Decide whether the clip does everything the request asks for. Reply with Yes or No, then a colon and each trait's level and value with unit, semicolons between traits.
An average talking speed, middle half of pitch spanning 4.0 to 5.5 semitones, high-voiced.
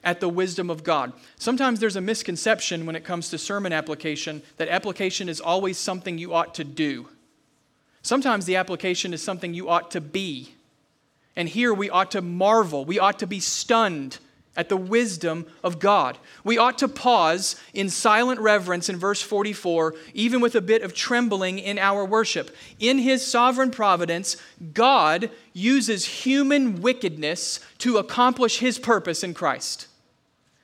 Yes: average, 160 wpm; average, 4.8 semitones; high, 195 Hz